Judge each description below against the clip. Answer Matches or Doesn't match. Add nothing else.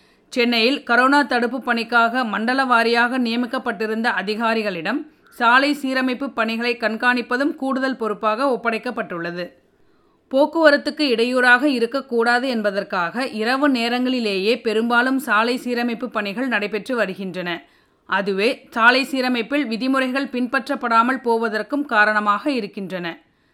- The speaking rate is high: Doesn't match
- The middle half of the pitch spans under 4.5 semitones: Matches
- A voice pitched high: Matches